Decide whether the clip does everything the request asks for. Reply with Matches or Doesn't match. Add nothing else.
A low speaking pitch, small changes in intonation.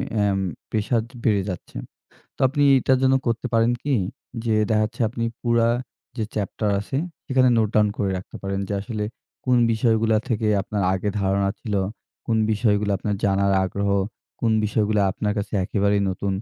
Matches